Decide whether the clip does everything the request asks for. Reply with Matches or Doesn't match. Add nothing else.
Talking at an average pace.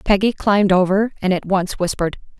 Matches